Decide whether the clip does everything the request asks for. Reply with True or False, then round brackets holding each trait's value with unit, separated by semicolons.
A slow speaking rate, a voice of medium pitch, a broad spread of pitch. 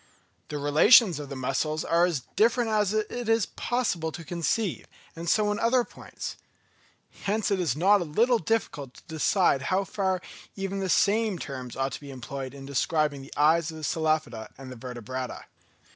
False (175 wpm; 165 Hz; 6.8 semitones)